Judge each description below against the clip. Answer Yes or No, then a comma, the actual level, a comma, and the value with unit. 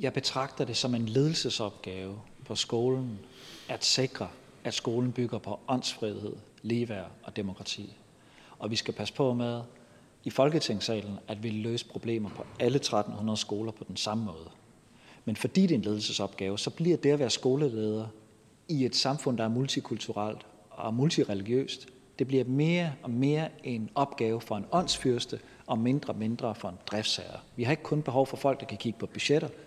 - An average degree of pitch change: Yes, average, 3.9 semitones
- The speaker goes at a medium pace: Yes, average, 175 wpm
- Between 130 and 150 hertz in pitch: No, low, 120 Hz